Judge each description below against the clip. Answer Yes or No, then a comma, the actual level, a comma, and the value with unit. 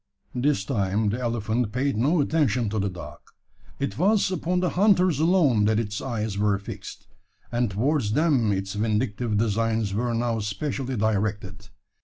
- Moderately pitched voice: No, low, 115 Hz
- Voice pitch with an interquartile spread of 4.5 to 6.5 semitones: Yes, average, 5.1 semitones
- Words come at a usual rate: Yes, average, 155 wpm